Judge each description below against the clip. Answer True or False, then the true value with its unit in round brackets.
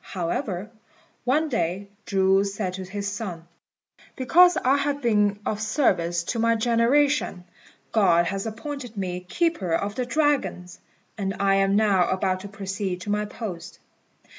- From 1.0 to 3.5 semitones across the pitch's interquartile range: False (4.1 semitones)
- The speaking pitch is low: False (205 Hz)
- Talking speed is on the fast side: False (145 wpm)